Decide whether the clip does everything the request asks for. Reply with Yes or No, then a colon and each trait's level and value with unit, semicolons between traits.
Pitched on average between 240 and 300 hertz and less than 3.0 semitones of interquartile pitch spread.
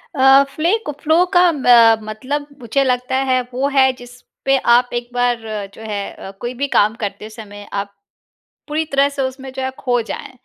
Yes: very high, 255 Hz; narrow, 2.6 semitones